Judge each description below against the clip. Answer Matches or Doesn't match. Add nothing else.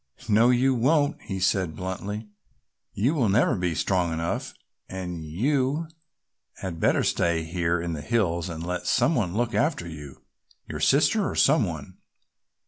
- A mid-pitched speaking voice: Doesn't match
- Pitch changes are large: Matches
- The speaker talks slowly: Doesn't match